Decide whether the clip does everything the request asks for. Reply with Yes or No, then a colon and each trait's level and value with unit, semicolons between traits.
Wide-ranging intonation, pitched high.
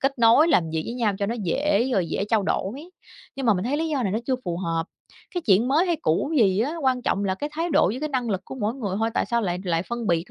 Yes: wide, 6.2 semitones; high, 230 Hz